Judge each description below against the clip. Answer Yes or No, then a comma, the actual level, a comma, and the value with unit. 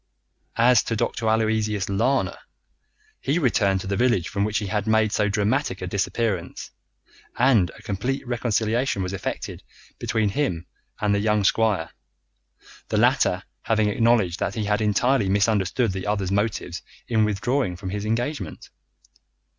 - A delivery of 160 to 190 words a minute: No, average, 145 wpm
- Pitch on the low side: Yes, low, 105 Hz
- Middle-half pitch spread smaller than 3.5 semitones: Yes, average, 2.9 semitones